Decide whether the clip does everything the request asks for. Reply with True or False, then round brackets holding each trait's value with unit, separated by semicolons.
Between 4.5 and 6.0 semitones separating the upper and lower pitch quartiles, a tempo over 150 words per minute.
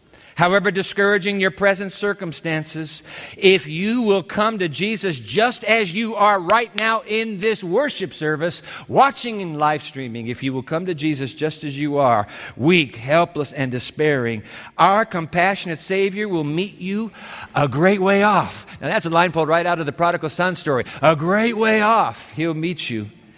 True (4.9 semitones; 175 wpm)